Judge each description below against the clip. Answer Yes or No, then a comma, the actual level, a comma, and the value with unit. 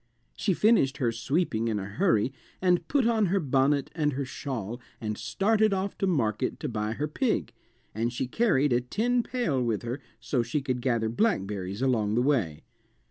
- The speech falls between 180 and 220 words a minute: Yes, average, 185 wpm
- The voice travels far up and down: Yes, wide, 8.0 semitones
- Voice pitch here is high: No, low, 130 Hz